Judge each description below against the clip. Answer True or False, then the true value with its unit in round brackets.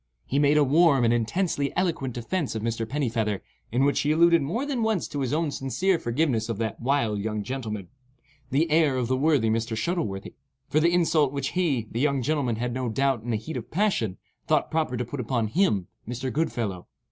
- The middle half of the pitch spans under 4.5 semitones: False (5.2 semitones)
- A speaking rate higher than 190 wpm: True (200 wpm)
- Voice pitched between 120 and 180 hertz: True (135 Hz)